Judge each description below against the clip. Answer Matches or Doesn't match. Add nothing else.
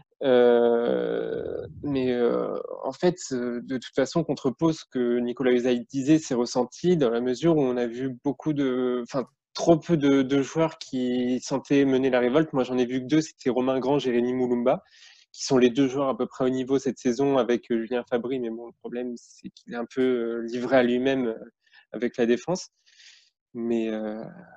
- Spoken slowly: Doesn't match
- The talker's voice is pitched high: Doesn't match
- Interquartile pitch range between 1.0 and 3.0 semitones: Matches